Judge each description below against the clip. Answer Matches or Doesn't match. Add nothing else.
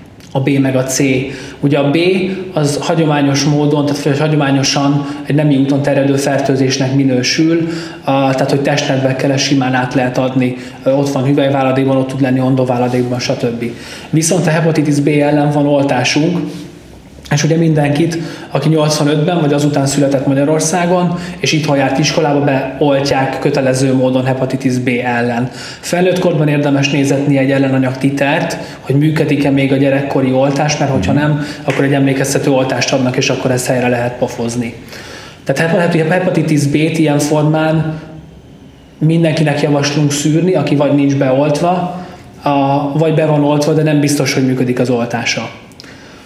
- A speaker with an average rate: Matches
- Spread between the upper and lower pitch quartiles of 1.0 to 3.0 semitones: Matches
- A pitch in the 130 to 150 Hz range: Matches